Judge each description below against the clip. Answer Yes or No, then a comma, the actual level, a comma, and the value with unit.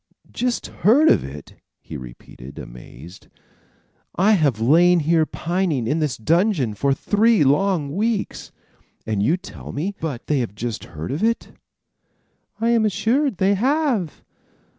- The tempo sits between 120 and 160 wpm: Yes, average, 140 wpm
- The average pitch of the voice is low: No, medium, 165 Hz